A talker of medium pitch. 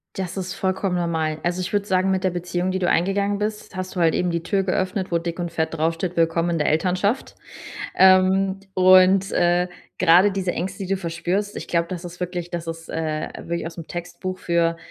Yes: medium, 180 Hz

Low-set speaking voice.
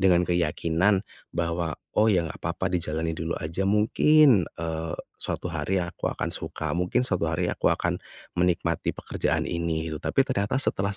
Yes: very low, 85 Hz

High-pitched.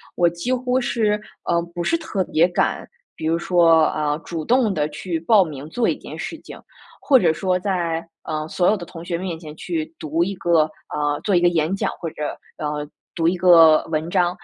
No: medium, 170 Hz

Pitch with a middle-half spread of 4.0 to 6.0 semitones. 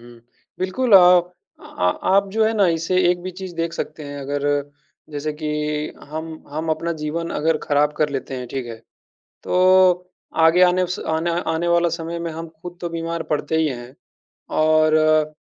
No: average, 2.7 semitones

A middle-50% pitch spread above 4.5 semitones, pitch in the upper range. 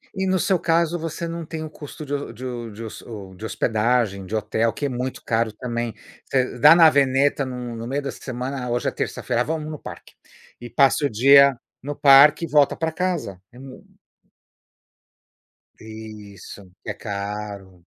No: average, 5.0 semitones; low, 130 Hz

